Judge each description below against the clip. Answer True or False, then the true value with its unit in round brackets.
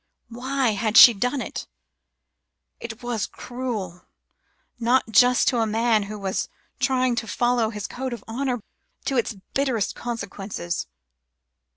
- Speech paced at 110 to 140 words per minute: True (135 wpm)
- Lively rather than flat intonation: False (2.8 semitones)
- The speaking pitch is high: True (235 Hz)